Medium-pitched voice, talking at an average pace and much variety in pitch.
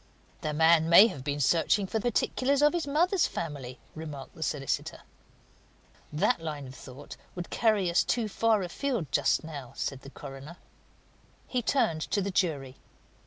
Yes: medium, 165 Hz; average, 160 wpm; wide, 7.5 semitones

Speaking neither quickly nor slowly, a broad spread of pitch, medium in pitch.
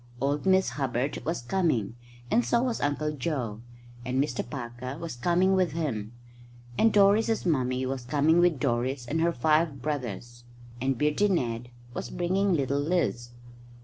Yes: average, 150 wpm; wide, 5.7 semitones; medium, 145 Hz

